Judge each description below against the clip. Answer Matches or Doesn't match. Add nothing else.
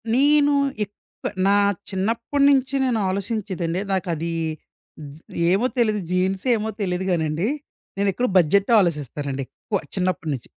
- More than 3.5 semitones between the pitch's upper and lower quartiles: Matches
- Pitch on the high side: Matches